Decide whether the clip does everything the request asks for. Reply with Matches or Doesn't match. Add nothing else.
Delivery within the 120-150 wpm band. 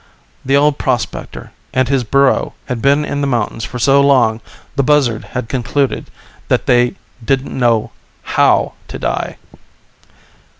Matches